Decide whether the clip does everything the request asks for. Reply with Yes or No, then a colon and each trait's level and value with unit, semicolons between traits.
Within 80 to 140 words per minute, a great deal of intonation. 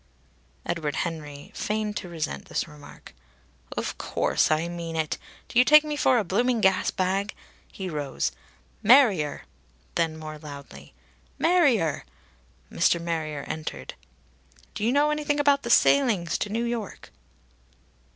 Yes: slow, 135 wpm; wide, 7.4 semitones